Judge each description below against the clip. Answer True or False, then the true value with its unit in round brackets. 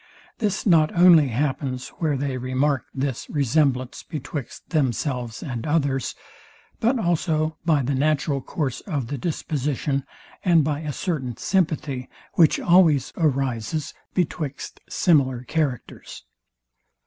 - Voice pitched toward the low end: False (145 Hz)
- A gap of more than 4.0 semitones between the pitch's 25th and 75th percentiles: False (3.4 semitones)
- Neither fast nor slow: False (115 wpm)